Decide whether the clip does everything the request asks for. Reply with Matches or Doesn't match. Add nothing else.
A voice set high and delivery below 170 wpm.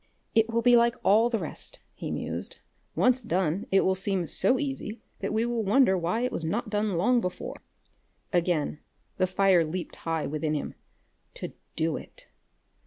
Doesn't match